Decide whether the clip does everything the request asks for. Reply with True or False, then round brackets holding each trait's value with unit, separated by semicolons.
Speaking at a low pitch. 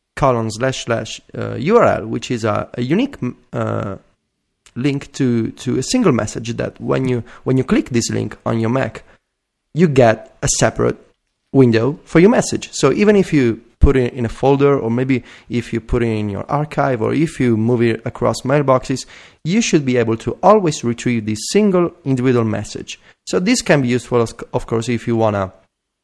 True (125 Hz)